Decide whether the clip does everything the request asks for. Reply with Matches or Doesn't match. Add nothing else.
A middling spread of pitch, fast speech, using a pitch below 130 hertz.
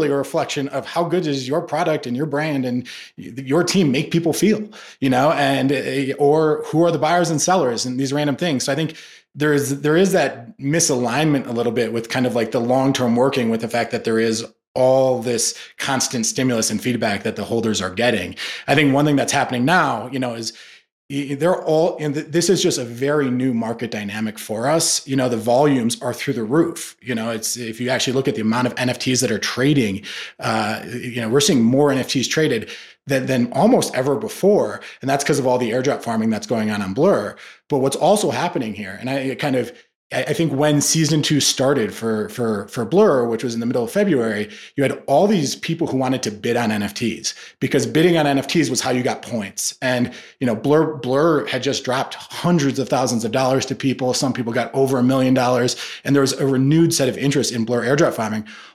Doesn't match